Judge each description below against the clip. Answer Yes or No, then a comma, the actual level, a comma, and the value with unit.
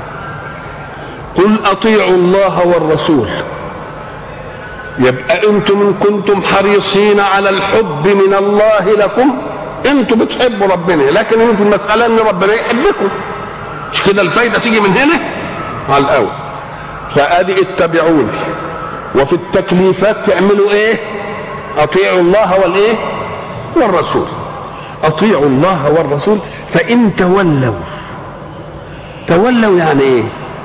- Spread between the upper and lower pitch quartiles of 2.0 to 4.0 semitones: Yes, average, 3.7 semitones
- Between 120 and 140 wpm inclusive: No, average, 95 wpm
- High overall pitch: Yes, high, 195 Hz